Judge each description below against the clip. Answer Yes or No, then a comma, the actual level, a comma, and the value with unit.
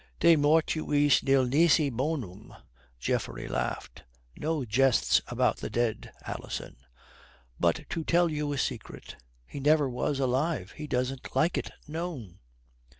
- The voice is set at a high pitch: No, medium, 140 Hz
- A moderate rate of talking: No, slow, 130 wpm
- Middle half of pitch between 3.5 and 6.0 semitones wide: Yes, average, 3.8 semitones